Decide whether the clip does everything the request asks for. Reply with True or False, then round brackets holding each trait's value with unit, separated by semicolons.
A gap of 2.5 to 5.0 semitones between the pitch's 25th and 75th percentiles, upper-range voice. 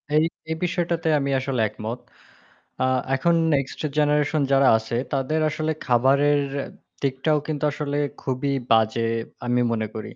False (3.5 semitones; 140 Hz)